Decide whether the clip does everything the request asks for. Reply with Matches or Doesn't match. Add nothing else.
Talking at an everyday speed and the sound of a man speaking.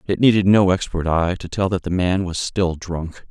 Doesn't match